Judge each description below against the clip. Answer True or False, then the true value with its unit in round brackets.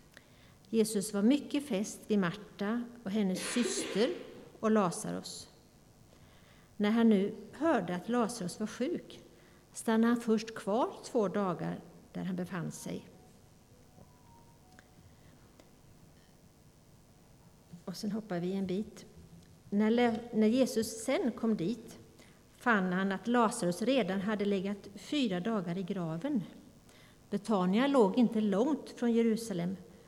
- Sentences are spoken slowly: True (115 wpm)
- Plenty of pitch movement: False (3.3 semitones)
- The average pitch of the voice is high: True (215 Hz)